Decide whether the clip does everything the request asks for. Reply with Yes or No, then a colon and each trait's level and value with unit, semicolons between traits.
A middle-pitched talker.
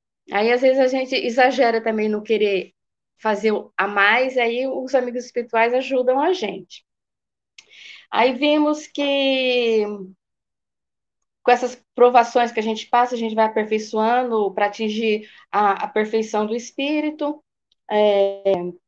No: high, 230 Hz